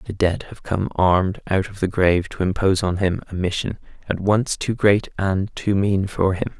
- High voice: No, very low, 95 Hz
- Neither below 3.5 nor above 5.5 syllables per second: Yes, 5.0 syllables/s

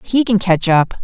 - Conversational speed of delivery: No, fast, 230 wpm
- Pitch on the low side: No, high, 195 Hz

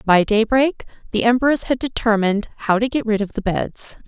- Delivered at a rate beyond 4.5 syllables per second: Yes, 5.2 syllables/s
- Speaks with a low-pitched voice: No, high, 225 Hz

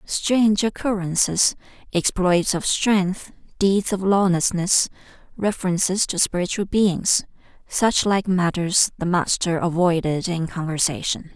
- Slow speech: Yes, slow, 100 wpm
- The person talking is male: No, female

